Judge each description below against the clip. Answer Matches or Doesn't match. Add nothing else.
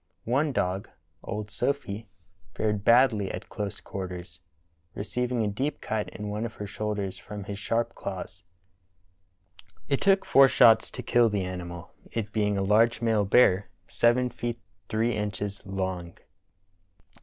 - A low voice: Matches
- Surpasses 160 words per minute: Doesn't match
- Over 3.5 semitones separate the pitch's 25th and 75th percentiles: Doesn't match